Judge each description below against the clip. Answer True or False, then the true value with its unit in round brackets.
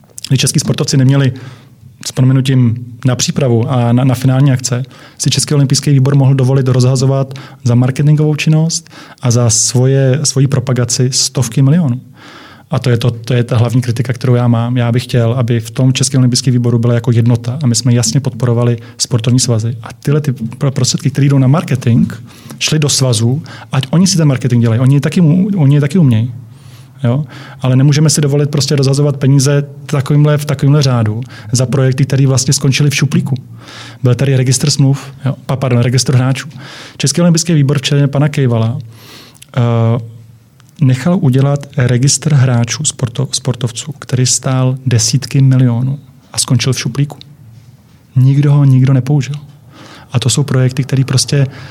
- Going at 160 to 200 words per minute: True (165 wpm)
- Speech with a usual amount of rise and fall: False (2.3 semitones)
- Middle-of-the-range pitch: False (130 Hz)